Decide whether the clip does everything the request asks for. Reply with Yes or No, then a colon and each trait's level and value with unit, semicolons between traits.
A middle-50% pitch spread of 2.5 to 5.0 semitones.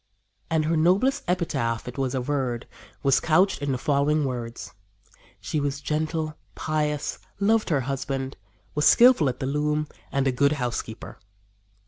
Yes: average, 2.8 semitones